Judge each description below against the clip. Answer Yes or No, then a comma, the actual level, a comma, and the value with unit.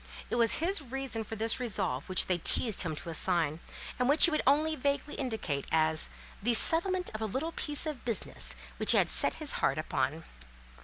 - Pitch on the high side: Yes, high, 235 Hz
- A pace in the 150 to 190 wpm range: No, average, 200 wpm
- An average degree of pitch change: No, wide, 8.1 semitones